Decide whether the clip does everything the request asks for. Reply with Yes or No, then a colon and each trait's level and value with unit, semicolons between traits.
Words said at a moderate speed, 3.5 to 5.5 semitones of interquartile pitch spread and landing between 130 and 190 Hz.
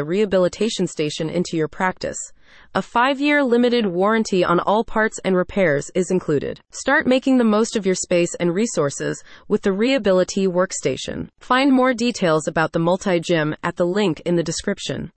Yes: average, 165 wpm; average, 4.5 semitones; medium, 185 Hz